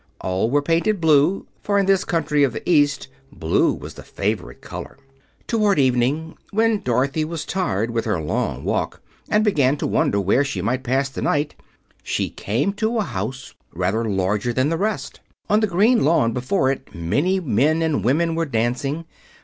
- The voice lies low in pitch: No, medium, 145 Hz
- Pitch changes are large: Yes, wide, 7.0 semitones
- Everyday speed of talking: Yes, average, 180 wpm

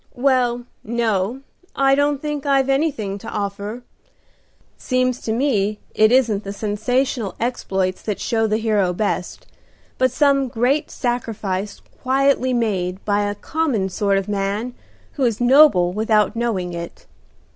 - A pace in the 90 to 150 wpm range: Yes, slow, 135 wpm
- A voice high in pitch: Yes, high, 225 Hz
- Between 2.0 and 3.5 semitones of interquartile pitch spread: No, average, 4.2 semitones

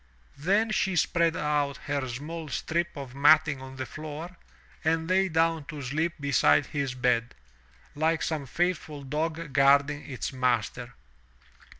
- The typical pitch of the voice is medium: Yes, medium, 150 Hz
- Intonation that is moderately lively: Yes, average, 3.4 semitones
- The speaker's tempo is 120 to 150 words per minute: Yes, slow, 135 wpm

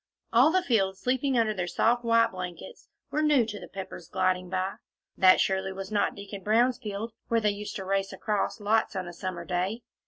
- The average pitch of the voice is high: Yes, high, 205 Hz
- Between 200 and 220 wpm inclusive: Yes, fast, 205 wpm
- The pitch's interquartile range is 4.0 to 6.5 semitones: No, average, 3.5 semitones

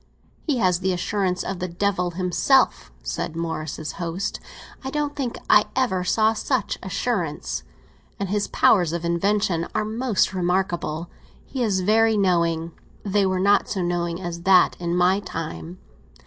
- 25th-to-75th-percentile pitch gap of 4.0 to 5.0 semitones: No, average, 3.3 semitones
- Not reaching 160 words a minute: Yes, average, 150 wpm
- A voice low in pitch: No, medium, 185 Hz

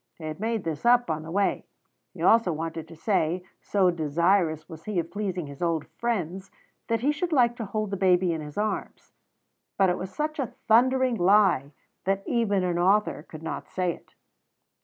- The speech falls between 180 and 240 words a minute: Yes, average, 195 wpm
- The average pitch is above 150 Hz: Yes, medium, 185 Hz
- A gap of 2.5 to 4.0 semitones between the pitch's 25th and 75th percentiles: No, average, 4.8 semitones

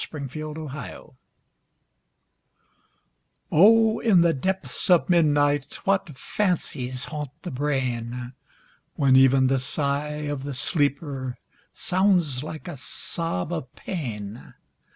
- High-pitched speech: No, medium, 145 Hz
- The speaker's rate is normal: No, slow, 110 wpm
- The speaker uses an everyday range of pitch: Yes, average, 4.6 semitones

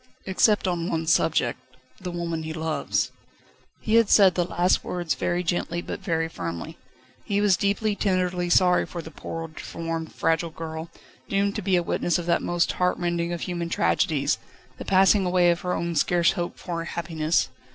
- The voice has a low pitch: No, medium, 175 Hz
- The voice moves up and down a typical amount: No, narrow, 1.8 semitones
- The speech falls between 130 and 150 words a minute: No, average, 175 wpm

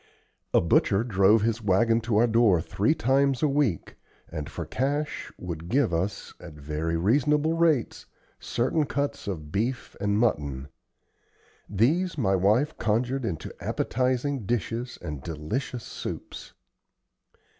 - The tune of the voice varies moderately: No, wide, 6.3 semitones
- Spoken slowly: Yes, slow, 130 wpm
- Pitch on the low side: Yes, low, 115 Hz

